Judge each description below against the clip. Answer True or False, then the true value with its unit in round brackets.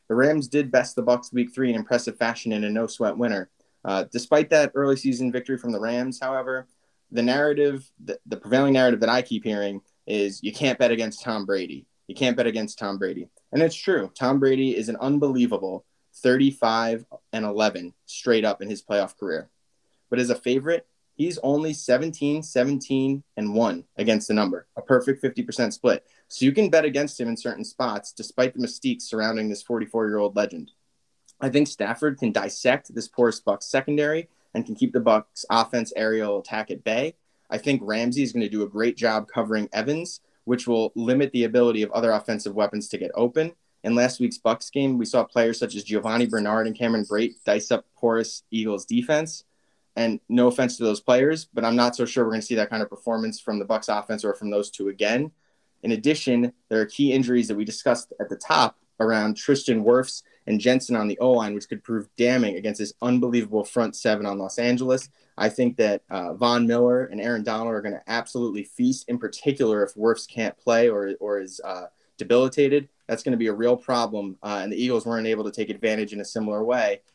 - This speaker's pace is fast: True (210 wpm)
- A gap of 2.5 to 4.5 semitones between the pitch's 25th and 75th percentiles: True (3.2 semitones)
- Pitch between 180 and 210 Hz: False (120 Hz)